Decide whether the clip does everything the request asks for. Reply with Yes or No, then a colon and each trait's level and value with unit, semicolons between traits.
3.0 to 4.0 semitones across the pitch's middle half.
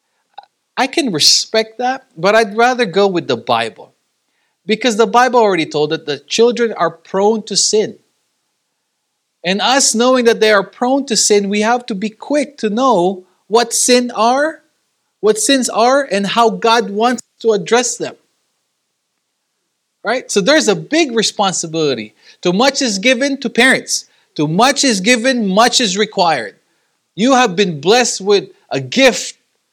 Yes: average, 3.7 semitones